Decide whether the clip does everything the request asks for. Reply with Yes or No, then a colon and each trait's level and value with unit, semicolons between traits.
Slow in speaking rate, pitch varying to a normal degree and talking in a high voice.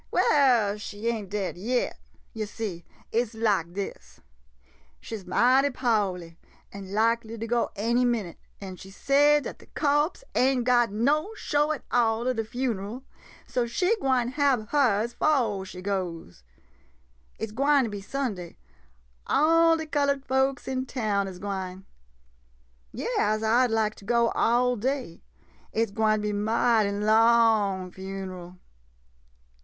No: average, 150 wpm; average, 4.4 semitones; high, 225 Hz